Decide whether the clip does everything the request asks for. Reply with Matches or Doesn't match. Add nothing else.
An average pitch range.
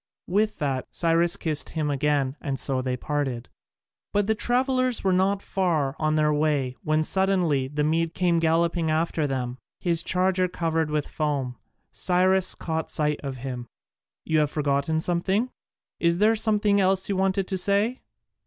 Matches